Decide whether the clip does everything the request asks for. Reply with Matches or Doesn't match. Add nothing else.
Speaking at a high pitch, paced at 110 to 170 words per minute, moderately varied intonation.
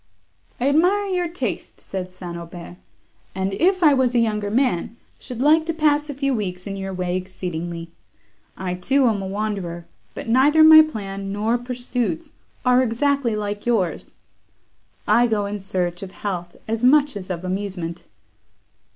Doesn't match